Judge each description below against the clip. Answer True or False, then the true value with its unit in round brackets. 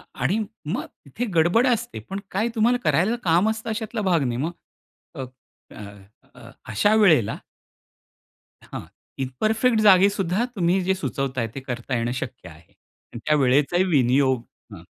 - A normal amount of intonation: False (8.6 semitones)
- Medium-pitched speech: True (175 Hz)